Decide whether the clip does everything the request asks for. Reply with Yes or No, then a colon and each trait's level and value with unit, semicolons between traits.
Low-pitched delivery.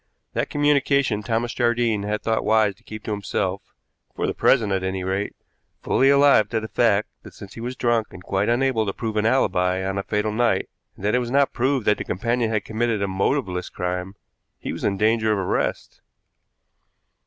Yes: low, 110 Hz